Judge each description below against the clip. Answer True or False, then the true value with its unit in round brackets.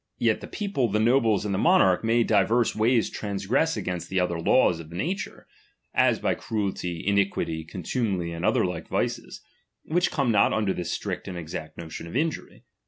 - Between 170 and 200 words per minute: True (180 wpm)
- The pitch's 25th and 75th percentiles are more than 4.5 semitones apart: True (5.2 semitones)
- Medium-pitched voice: False (100 Hz)